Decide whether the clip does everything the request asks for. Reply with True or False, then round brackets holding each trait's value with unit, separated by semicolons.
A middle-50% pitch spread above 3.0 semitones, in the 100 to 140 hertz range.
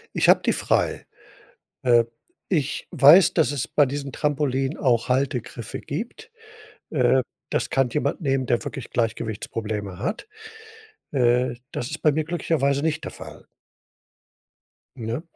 True (3.7 semitones; 135 Hz)